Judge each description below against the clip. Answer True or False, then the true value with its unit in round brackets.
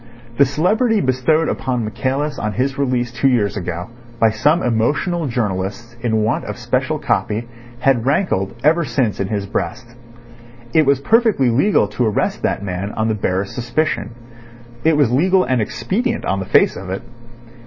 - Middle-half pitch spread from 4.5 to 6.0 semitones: True (5.6 semitones)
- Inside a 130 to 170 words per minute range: True (165 wpm)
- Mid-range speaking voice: False (125 Hz)